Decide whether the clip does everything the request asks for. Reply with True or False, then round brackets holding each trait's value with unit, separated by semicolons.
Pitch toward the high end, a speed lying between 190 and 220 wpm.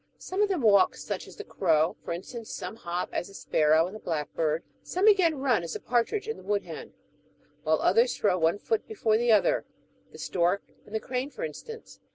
True (215 Hz; 205 wpm)